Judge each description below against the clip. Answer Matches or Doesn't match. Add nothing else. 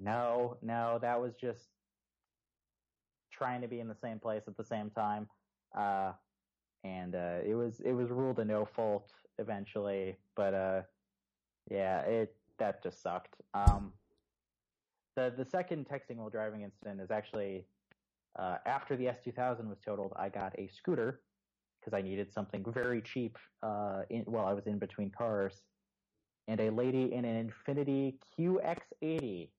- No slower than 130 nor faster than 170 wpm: Matches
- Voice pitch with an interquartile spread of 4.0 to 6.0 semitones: Doesn't match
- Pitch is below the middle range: Matches